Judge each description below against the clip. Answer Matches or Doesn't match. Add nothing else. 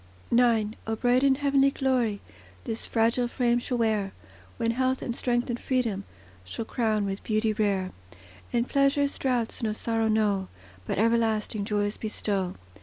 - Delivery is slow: Doesn't match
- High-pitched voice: Matches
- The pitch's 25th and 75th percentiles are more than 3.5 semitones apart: Doesn't match